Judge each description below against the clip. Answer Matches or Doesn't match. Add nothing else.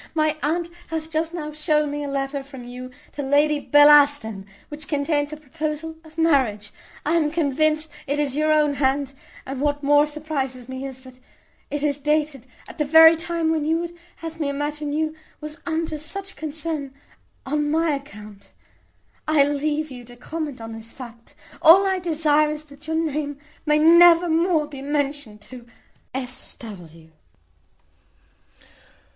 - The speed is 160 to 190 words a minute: Matches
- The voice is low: Doesn't match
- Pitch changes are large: Doesn't match